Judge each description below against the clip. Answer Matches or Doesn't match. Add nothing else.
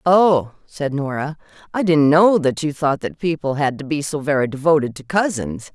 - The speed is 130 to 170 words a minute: Doesn't match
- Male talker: Doesn't match